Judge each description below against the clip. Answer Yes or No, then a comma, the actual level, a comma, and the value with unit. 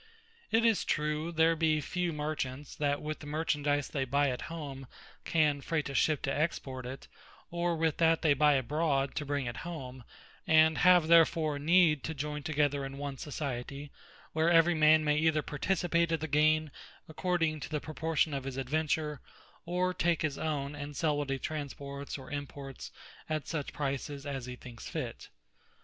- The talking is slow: No, average, 175 wpm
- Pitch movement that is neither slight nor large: No, narrow, 2.3 semitones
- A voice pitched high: No, medium, 150 Hz